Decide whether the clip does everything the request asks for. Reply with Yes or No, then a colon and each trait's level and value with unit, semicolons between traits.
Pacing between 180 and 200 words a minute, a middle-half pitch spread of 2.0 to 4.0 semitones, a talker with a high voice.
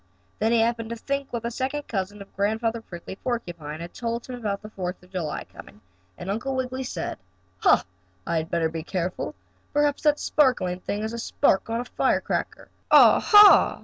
No: average, 185 wpm; wide, 5.4 semitones; high, 225 Hz